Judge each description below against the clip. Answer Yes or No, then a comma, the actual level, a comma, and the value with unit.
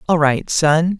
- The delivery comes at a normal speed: Yes, average, 180 wpm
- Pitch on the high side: No, medium, 160 Hz